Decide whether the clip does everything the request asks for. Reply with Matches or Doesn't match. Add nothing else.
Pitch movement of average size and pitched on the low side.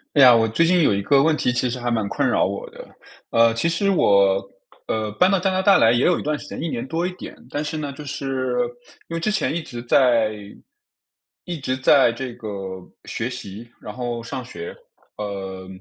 Doesn't match